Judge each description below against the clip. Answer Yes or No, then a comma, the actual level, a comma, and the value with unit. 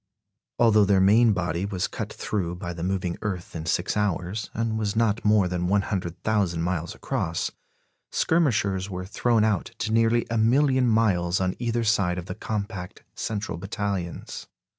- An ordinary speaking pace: Yes, average, 160 wpm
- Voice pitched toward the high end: No, low, 100 Hz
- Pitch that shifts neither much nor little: Yes, average, 3.7 semitones